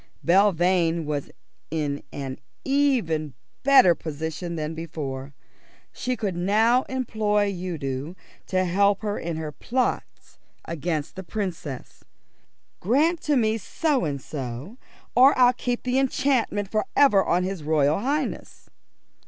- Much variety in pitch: Yes, wide, 7.3 semitones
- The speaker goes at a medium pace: No, slow, 125 wpm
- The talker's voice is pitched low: No, medium, 185 Hz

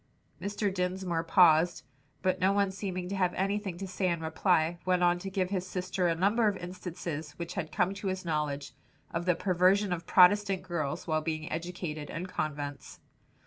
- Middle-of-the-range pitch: Yes, medium, 180 Hz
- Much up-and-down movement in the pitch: No, narrow, 2.5 semitones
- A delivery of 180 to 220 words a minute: Yes, average, 185 wpm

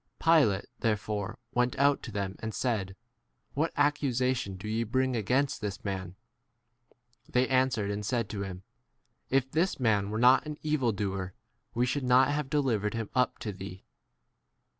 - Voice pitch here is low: Yes, low, 115 Hz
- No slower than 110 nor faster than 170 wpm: Yes, average, 160 wpm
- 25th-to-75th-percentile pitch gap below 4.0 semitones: No, average, 4.5 semitones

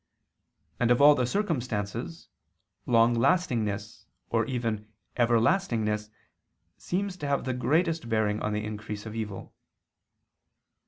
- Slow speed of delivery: Yes, slow, 110 wpm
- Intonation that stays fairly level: No, average, 5.2 semitones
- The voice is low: Yes, low, 120 Hz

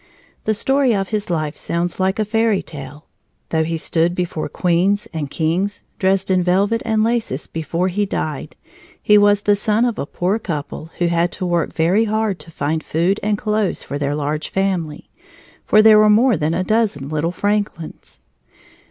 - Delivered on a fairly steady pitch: No, average, 4.5 semitones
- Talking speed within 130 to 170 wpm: No, average, 180 wpm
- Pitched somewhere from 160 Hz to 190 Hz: Yes, medium, 185 Hz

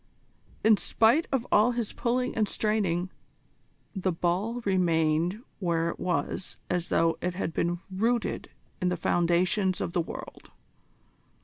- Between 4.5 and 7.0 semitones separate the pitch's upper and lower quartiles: No, average, 4.1 semitones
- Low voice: No, medium, 185 Hz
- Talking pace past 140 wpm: No, slow, 135 wpm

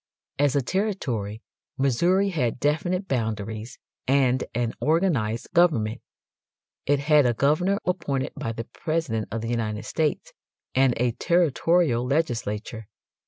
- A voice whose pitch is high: No, low, 135 Hz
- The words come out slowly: Yes, slow, 120 wpm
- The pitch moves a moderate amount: No, wide, 6.2 semitones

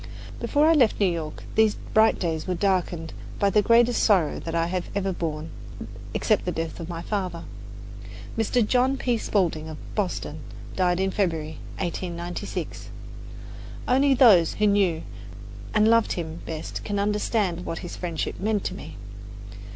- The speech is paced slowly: No, average, 155 wpm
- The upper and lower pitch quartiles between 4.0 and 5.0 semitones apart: Yes, average, 4.3 semitones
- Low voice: No, medium, 185 Hz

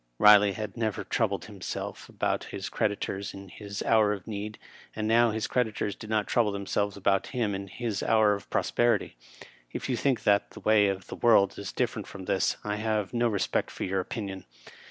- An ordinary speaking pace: Yes, average, 195 wpm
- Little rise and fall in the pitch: Yes, narrow, 1.9 semitones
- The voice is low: Yes, low, 105 Hz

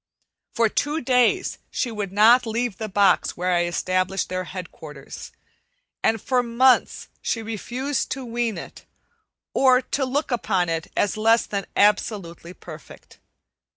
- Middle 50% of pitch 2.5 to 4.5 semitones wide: No, average, 5.1 semitones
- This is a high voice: Yes, high, 220 Hz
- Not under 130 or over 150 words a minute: Yes, average, 140 wpm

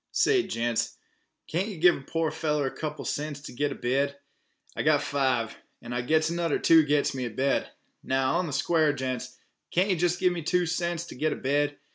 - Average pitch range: Yes, average, 4.2 semitones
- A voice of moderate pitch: Yes, medium, 150 Hz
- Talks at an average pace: No, fast, 220 wpm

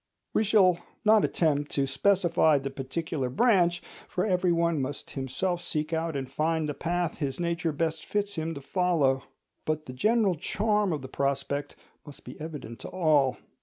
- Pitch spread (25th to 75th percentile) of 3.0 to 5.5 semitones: Yes, average, 4.3 semitones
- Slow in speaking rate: No, average, 165 wpm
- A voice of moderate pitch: Yes, medium, 160 Hz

